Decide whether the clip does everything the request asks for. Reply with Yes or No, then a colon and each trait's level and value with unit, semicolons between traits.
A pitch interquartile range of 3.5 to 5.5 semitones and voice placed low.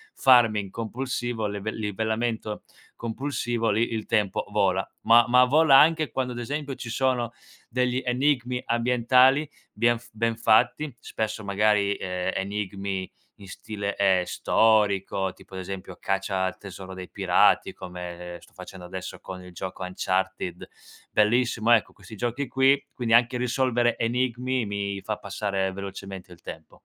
Yes: average, 4.1 semitones; low, 110 Hz